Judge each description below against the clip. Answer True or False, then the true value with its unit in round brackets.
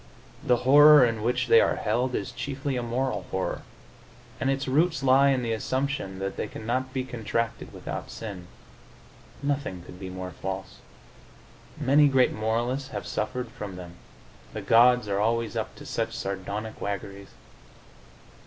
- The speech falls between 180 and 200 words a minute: False (155 wpm)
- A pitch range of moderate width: True (4.6 semitones)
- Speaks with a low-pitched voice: True (120 Hz)